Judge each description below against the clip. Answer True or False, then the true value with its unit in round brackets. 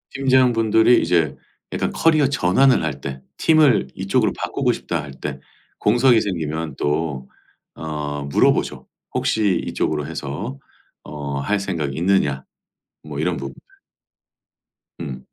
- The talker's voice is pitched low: True (80 Hz)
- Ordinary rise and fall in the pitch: False (7.6 semitones)